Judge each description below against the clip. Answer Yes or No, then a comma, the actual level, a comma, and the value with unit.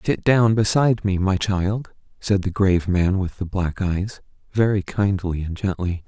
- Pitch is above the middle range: No, very low, 95 Hz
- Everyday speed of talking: Yes, average, 180 wpm